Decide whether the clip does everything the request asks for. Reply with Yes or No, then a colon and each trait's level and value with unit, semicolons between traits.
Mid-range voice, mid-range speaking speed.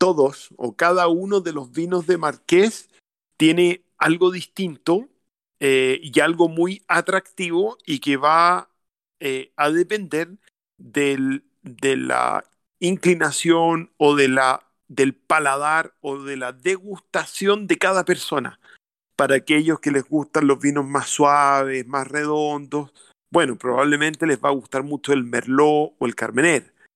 Yes: medium, 150 Hz; average, 140 wpm